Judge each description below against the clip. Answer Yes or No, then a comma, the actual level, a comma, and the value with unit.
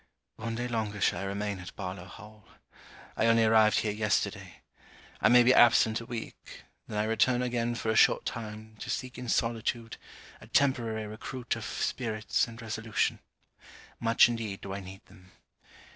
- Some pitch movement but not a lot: No, narrow, 1.8 semitones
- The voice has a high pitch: No, low, 110 Hz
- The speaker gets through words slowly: No, average, 170 wpm